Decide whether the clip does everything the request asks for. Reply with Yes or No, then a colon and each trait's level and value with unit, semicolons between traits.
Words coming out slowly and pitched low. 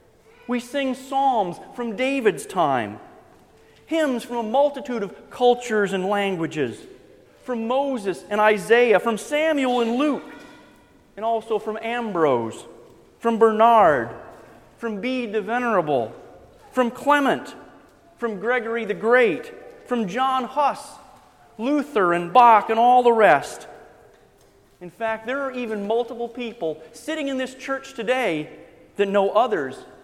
No: slow, 125 wpm; high, 235 Hz